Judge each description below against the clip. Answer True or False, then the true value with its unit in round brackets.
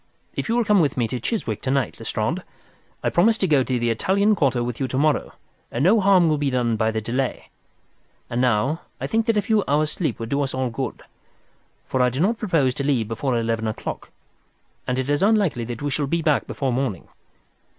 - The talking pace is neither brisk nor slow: False (225 wpm)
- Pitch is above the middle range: False (135 Hz)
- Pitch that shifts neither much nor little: False (6.1 semitones)